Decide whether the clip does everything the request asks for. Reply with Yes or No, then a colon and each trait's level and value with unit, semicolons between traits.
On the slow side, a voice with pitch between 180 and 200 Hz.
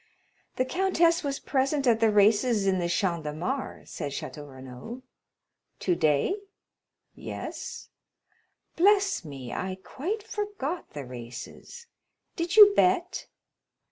No: slow, 115 wpm; high, 245 Hz